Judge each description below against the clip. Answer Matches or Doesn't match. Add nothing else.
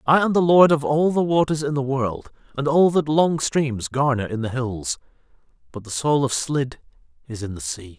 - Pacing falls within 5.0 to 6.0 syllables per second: Doesn't match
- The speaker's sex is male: Matches